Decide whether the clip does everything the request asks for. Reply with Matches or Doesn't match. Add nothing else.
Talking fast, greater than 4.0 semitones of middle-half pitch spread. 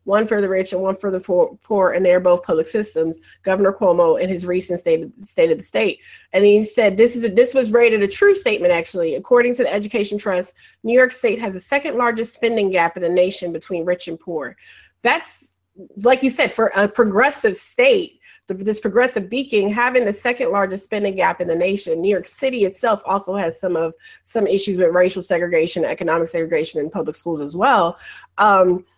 Matches